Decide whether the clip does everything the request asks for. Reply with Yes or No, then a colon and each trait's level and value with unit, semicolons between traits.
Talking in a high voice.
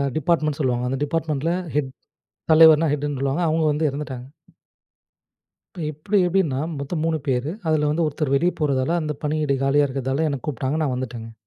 No: medium, 150 Hz